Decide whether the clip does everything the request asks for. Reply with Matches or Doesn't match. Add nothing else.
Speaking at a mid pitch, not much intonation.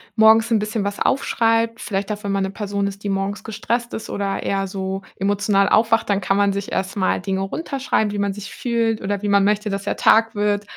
Doesn't match